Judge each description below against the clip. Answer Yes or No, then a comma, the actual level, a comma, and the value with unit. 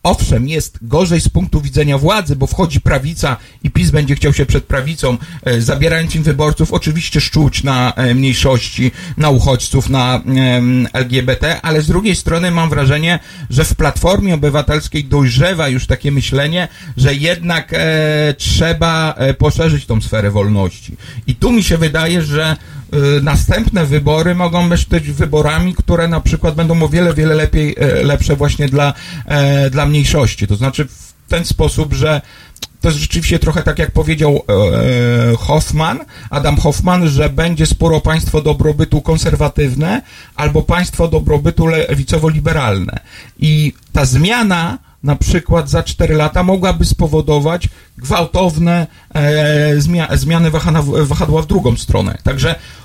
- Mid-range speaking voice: Yes, medium, 150 Hz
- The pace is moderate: Yes, average, 135 wpm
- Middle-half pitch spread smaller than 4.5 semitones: Yes, average, 3.6 semitones